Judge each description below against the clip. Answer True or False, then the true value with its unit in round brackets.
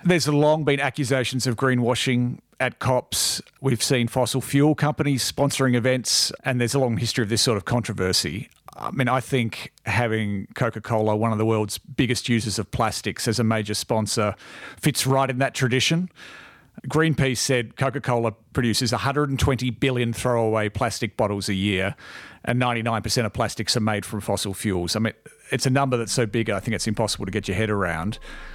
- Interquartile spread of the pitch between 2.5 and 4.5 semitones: True (3.5 semitones)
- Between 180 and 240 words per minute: True (185 wpm)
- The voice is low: True (120 Hz)